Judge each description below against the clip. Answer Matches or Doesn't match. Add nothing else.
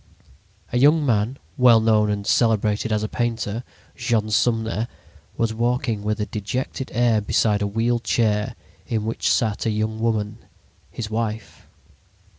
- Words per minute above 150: Doesn't match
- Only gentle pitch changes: Matches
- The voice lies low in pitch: Matches